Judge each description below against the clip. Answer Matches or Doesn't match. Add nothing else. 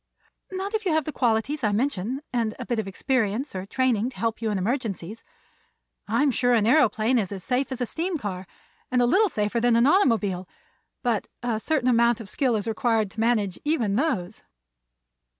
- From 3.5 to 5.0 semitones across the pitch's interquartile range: Matches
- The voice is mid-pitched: Doesn't match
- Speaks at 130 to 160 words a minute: Doesn't match